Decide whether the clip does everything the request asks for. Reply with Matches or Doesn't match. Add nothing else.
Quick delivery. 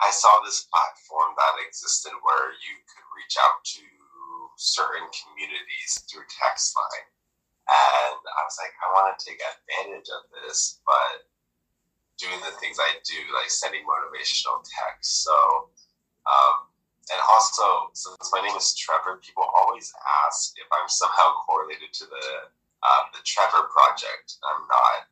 Doesn't match